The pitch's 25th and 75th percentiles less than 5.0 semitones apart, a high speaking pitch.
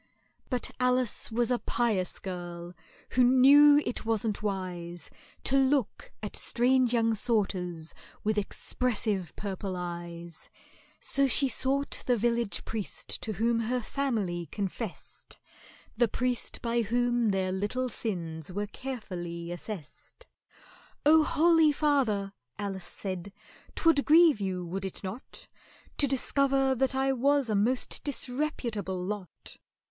No: wide, 5.4 semitones; high, 225 Hz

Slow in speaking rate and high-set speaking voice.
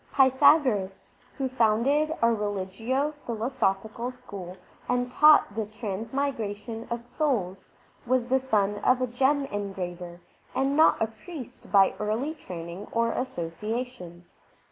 Yes: slow, 120 wpm; high, 230 Hz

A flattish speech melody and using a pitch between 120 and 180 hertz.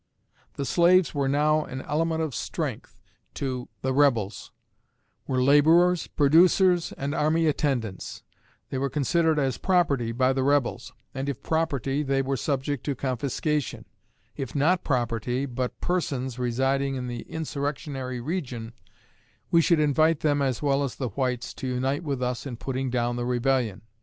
No: average, 3.2 semitones; low, 135 Hz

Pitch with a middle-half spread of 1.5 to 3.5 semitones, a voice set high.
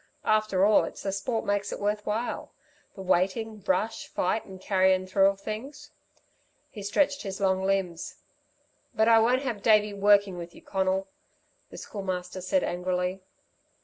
Yes: narrow, 2.4 semitones; high, 195 Hz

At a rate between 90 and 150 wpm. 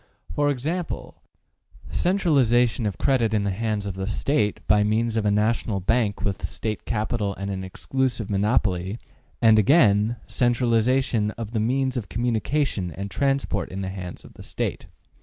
No: average, 160 wpm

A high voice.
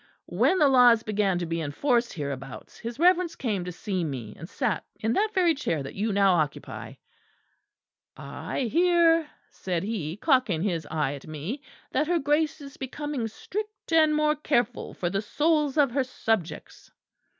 Yes: high, 235 Hz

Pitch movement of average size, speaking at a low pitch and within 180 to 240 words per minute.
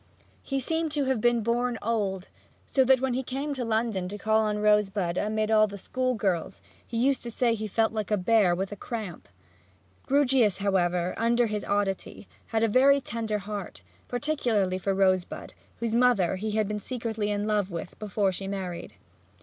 No: average, 3.5 semitones; high, 215 Hz; average, 185 wpm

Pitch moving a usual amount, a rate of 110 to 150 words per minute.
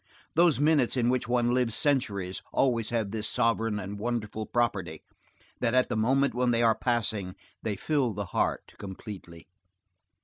No: average, 3.2 semitones; average, 160 wpm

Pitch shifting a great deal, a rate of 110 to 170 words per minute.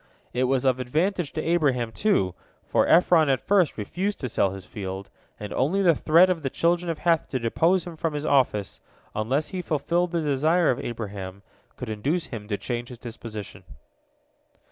No: wide, 7.0 semitones; average, 185 wpm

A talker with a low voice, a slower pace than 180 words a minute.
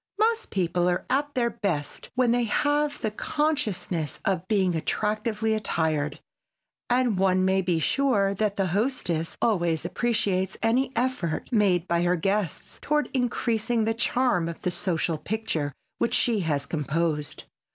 No: high, 200 Hz; average, 145 wpm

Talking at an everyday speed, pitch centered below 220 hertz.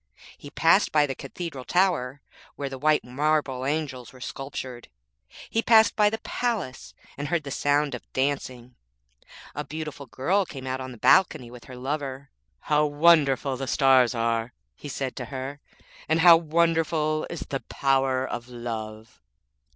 Yes: average, 155 wpm; medium, 140 Hz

